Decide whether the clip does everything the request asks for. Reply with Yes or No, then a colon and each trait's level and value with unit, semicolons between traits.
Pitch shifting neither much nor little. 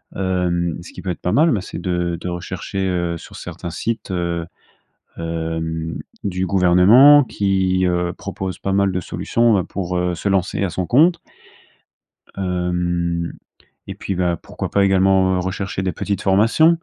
No: narrow, 2.0 semitones